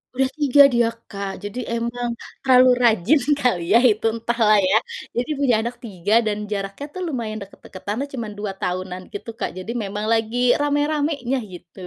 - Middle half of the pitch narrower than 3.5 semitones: No, average, 3.9 semitones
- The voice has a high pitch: Yes, high, 230 Hz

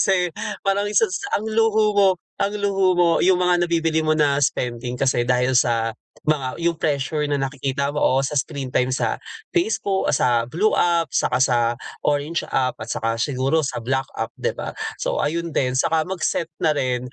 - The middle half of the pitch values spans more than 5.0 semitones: Yes, wide, 5.5 semitones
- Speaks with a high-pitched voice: No, medium, 150 Hz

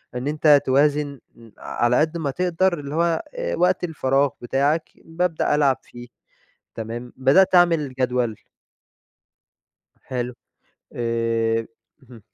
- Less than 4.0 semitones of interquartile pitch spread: No, average, 4.7 semitones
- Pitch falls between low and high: Yes, medium, 145 Hz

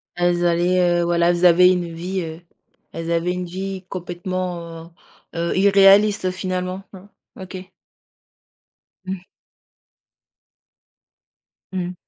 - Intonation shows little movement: Yes, narrow, 1.3 semitones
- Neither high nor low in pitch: Yes, medium, 180 Hz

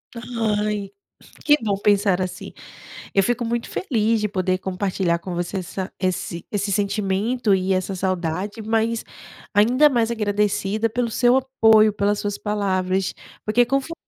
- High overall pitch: Yes, high, 205 Hz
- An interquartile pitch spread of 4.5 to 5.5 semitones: No, average, 3.2 semitones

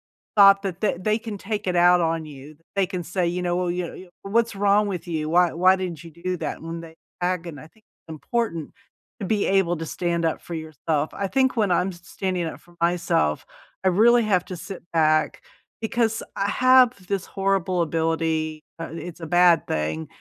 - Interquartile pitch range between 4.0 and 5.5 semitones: No, average, 3.2 semitones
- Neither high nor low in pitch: Yes, medium, 180 Hz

